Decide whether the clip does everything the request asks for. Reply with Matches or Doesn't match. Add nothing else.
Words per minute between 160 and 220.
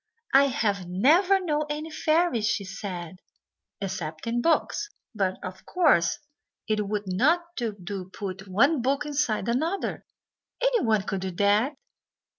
Doesn't match